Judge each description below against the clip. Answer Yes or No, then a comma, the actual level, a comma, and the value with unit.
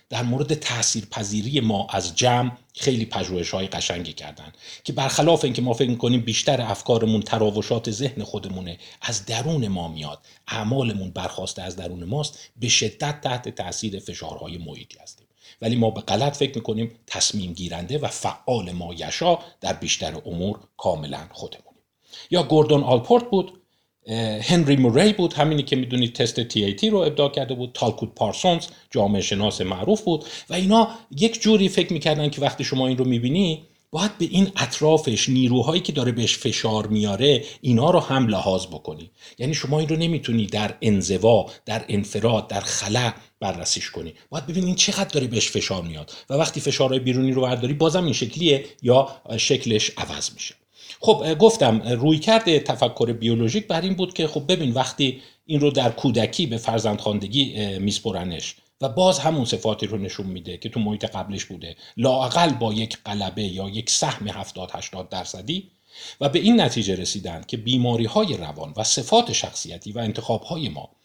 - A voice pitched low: Yes, low, 120 Hz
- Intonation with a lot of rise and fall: Yes, wide, 5.8 semitones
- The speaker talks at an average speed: No, fast, 165 wpm